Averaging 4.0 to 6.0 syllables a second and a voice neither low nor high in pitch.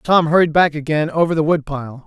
Yes: 5.4 syllables/s; medium, 155 Hz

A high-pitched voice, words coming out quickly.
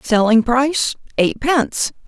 No: very high, 255 Hz; slow, 85 wpm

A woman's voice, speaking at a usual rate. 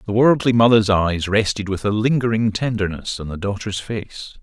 No: male; average, 175 wpm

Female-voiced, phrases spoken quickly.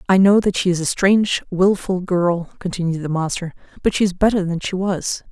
Yes: female; fast, 215 wpm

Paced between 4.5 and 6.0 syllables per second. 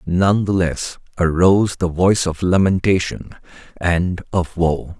No: 4.1 syllables/s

